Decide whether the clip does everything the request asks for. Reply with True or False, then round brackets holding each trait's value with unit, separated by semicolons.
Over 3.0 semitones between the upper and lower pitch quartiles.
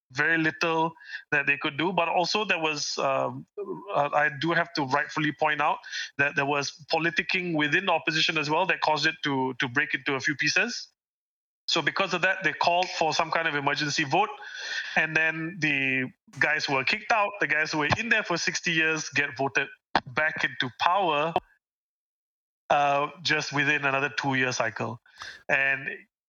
False (2.6 semitones)